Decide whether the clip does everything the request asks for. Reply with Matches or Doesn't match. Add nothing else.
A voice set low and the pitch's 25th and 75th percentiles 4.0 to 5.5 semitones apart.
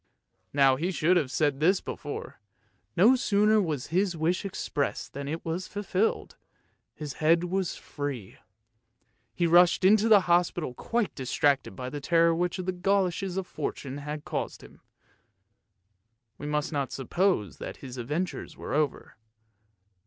Doesn't match